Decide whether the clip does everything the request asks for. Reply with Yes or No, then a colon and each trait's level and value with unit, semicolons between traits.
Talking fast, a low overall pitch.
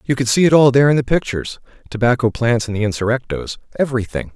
No: average, 180 wpm; low, 125 Hz